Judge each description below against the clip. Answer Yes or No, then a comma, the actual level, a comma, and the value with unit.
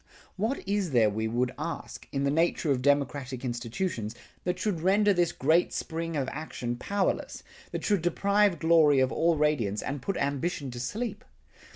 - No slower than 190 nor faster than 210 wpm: No, average, 170 wpm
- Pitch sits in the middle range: Yes, medium, 150 Hz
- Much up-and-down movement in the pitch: Yes, wide, 6.1 semitones